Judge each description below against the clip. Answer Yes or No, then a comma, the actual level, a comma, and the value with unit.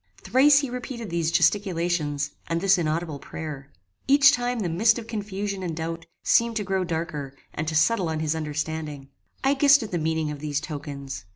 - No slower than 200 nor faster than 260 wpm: No, average, 185 wpm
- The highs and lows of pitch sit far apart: Yes, wide, 6.0 semitones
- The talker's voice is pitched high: No, medium, 165 Hz